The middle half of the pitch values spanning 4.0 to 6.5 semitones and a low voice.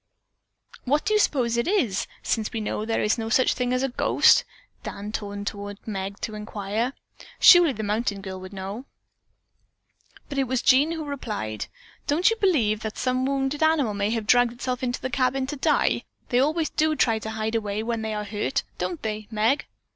No: average, 4.3 semitones; high, 235 Hz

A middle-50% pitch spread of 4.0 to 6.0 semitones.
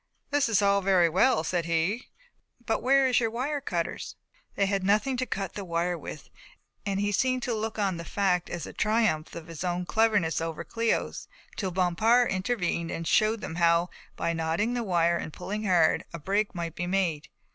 Yes: average, 4.6 semitones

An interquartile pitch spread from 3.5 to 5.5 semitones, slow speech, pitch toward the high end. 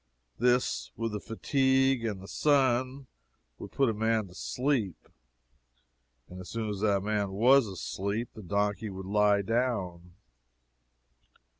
No: average, 4.0 semitones; slow, 125 wpm; low, 110 Hz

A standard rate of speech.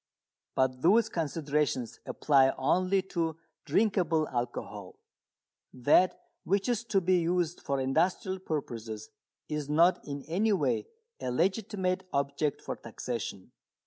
No: slow, 115 wpm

